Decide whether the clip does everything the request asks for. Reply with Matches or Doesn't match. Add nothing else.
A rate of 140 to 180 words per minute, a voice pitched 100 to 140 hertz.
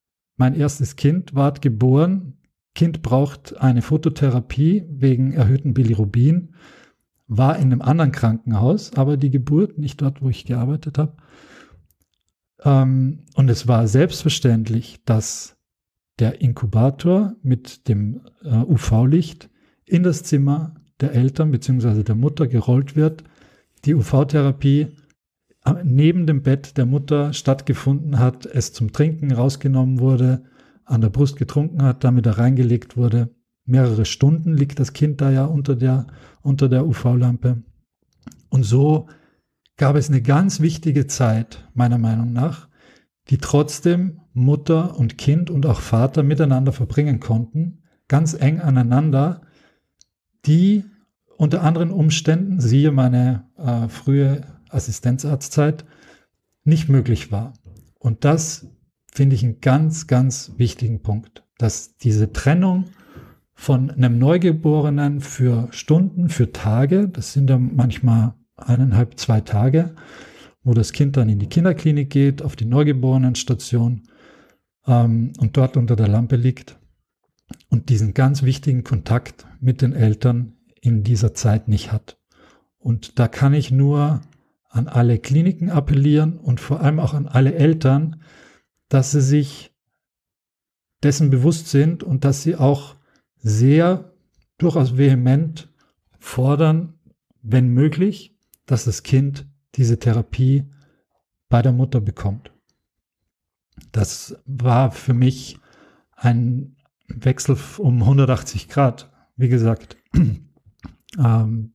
Doesn't match